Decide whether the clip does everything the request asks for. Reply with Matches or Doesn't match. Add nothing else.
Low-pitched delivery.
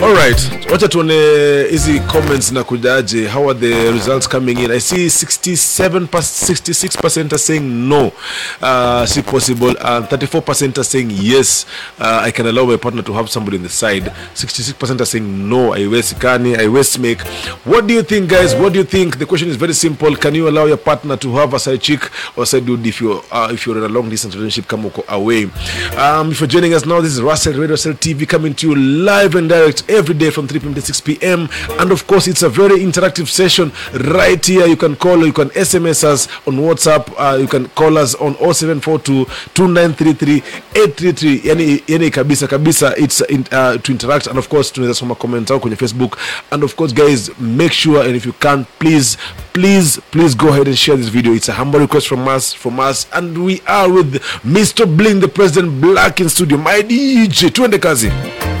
Doesn't match